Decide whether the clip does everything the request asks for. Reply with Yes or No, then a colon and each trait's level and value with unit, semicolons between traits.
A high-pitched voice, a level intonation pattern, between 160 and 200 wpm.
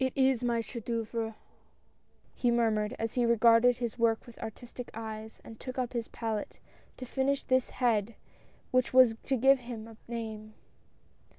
Yes: high, 235 Hz; narrow, 2.0 semitones; average, 175 wpm